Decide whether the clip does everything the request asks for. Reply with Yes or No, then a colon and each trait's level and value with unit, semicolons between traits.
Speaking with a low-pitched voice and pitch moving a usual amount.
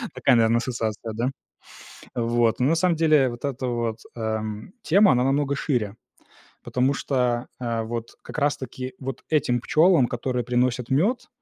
Yes: low, 125 Hz; average, 3.1 semitones